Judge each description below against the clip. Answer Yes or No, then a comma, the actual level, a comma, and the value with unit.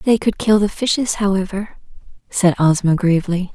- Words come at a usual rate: Yes, average, 150 wpm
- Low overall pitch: No, high, 195 Hz